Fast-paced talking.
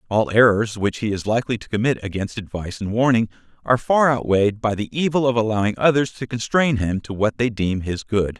Yes: fast, 215 wpm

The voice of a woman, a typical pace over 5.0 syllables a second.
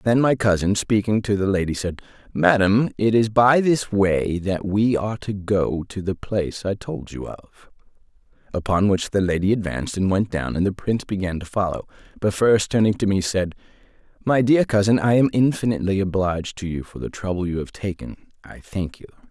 No: male; 5.3 syllables/s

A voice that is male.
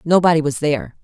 No: female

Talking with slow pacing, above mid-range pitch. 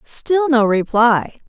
Yes: slow, 120 wpm; very high, 250 Hz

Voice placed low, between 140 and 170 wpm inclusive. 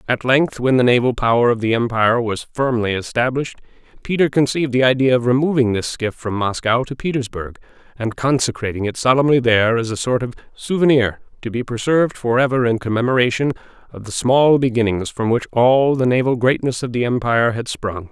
No: low, 120 Hz; average, 180 wpm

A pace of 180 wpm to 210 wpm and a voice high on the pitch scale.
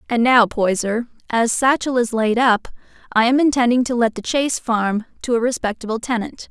Yes: average, 185 wpm; high, 235 Hz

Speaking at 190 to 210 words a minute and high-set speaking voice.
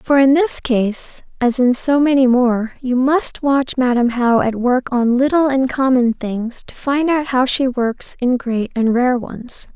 Yes: average, 195 wpm; very high, 255 Hz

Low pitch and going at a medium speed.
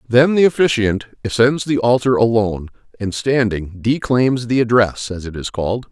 Yes: low, 115 Hz; average, 160 wpm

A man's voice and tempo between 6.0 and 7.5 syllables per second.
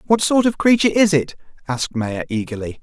Yes: male; 6.1 syllables/s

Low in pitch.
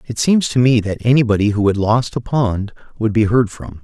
Yes: low, 115 Hz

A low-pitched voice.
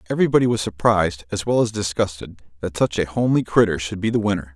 Yes: low, 100 Hz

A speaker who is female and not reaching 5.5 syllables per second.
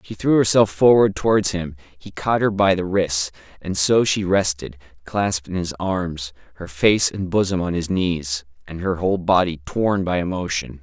No: male; 4.6 syllables/s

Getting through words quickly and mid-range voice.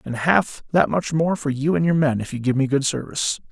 Yes: fast, 275 wpm; medium, 145 Hz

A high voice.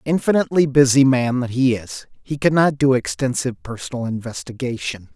No: low, 130 Hz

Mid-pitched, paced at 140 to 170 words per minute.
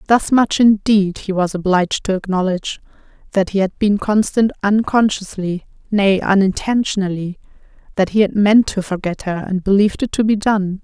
No: high, 200 Hz; average, 160 wpm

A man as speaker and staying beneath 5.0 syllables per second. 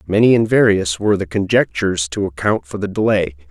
No: male; 5.9 syllables/s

